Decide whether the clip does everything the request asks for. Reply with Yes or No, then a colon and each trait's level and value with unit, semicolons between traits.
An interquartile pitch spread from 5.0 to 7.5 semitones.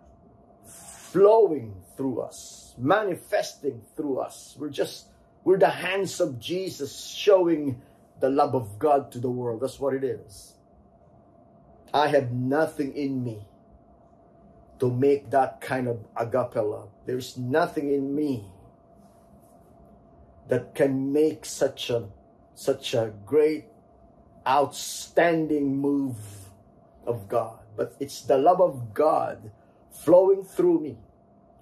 No: average, 4.3 semitones